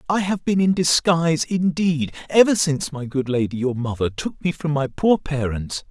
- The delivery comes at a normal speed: Yes, average, 195 wpm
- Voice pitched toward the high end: No, medium, 155 Hz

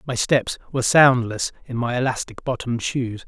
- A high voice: No, low, 125 Hz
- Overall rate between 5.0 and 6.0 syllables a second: Yes, 5.2 syllables/s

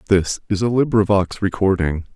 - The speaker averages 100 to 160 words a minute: Yes, average, 140 wpm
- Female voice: No, male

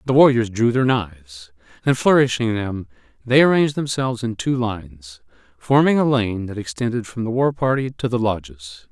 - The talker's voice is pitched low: Yes, low, 115 Hz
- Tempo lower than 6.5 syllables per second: Yes, 5.2 syllables/s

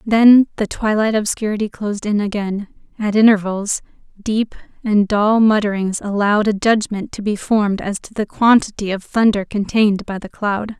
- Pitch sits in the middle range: No, high, 210 Hz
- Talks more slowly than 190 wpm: Yes, average, 160 wpm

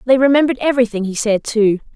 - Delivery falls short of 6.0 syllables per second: No, 7.0 syllables/s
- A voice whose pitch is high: Yes, high, 235 Hz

